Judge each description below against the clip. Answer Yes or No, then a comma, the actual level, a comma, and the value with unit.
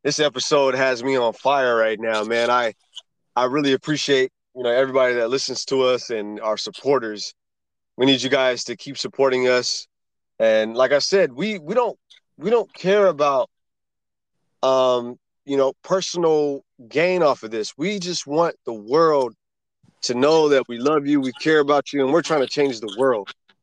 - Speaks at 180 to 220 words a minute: Yes, average, 185 wpm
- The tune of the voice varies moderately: Yes, average, 3.6 semitones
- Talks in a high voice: No, low, 135 Hz